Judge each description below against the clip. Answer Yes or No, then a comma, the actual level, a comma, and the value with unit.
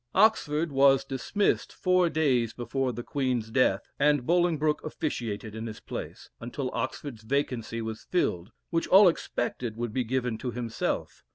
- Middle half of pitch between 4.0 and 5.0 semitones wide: Yes, average, 4.6 semitones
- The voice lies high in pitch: No, low, 130 Hz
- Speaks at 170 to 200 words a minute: No, average, 150 wpm